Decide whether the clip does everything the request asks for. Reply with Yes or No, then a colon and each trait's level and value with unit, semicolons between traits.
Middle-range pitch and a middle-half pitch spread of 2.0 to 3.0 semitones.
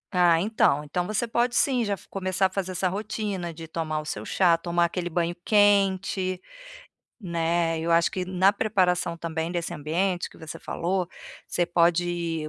Yes: medium, 175 Hz; narrow, 2.5 semitones